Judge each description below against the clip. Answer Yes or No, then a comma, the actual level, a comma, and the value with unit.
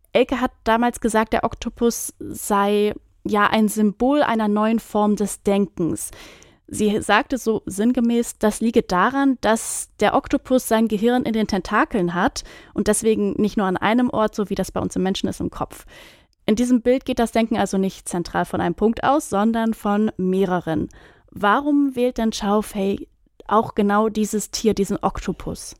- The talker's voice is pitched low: No, high, 215 Hz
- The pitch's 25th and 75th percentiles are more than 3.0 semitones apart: No, narrow, 2.6 semitones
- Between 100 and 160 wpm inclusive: No, average, 175 wpm